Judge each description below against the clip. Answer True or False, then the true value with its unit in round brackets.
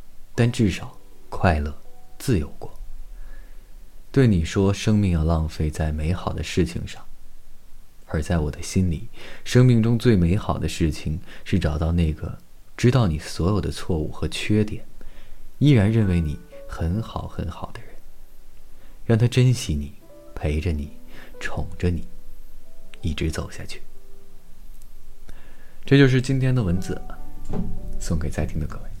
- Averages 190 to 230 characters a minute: True (200 characters per minute)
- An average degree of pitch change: True (4.7 semitones)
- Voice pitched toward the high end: False (90 Hz)